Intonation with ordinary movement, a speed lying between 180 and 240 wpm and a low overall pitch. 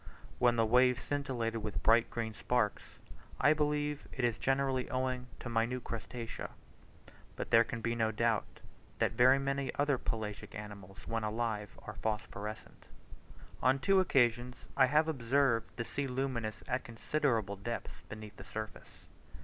No: average, 3.3 semitones; average, 150 wpm; low, 120 Hz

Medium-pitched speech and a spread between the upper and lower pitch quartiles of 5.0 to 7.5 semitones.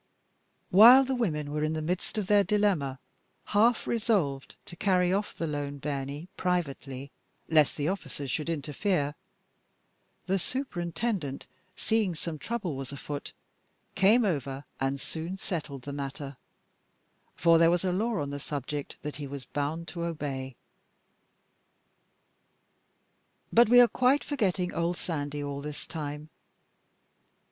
Yes: medium, 160 Hz; average, 5.3 semitones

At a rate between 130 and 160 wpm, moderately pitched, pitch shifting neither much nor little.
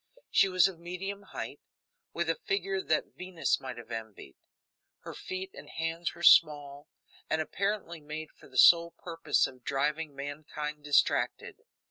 Yes: average, 150 wpm; medium, 160 Hz; average, 4.1 semitones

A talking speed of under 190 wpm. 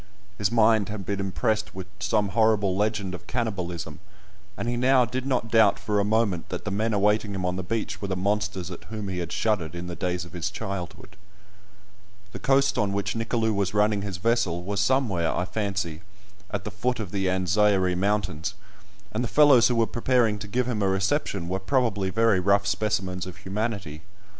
No: average, 195 wpm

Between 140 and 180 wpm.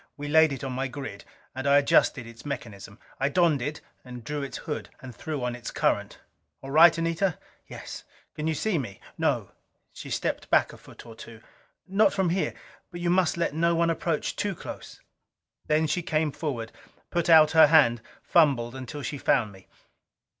No: average, 190 wpm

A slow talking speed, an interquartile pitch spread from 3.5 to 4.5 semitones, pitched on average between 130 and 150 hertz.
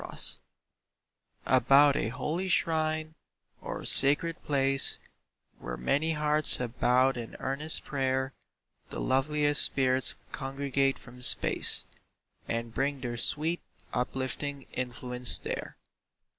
No: slow, 105 wpm; average, 2.8 semitones; low, 135 Hz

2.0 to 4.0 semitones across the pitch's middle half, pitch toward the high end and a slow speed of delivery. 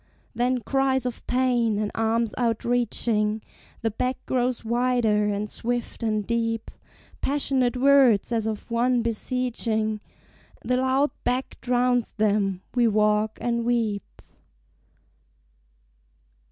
Yes: narrow, 2.5 semitones; high, 235 Hz; slow, 110 wpm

